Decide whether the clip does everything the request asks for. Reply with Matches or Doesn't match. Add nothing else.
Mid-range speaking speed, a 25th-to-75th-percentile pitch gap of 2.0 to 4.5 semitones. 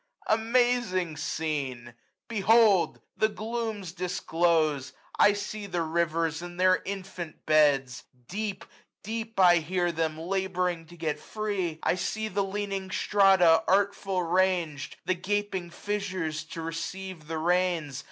Doesn't match